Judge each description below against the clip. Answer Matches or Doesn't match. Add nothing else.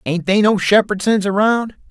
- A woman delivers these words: Doesn't match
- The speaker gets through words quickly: Doesn't match